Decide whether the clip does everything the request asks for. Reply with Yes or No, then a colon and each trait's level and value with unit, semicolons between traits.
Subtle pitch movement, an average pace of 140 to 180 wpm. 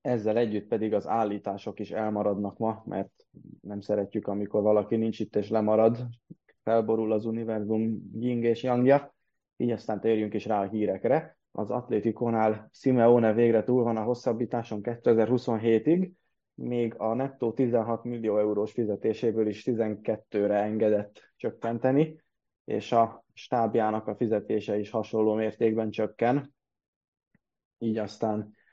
No: narrow, 1.8 semitones; average, 125 wpm